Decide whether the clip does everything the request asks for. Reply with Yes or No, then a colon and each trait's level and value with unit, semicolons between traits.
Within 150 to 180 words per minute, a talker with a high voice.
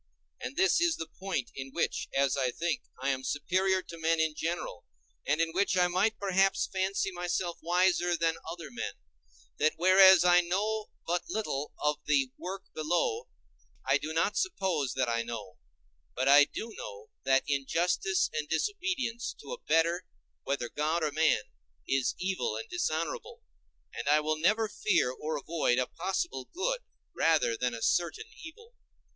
No: average, 165 wpm; medium, 170 Hz